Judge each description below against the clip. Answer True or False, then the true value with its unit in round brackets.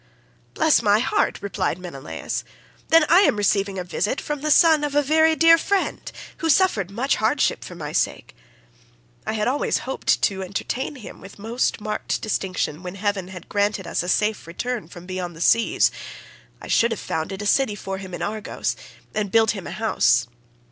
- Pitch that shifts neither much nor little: False (6.1 semitones)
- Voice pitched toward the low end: False (210 Hz)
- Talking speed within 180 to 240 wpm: True (185 wpm)